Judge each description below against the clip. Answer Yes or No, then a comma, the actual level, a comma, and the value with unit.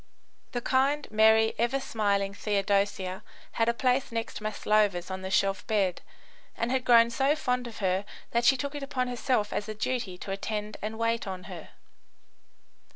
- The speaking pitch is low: No, high, 220 Hz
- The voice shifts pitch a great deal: No, average, 3.8 semitones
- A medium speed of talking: Yes, average, 170 wpm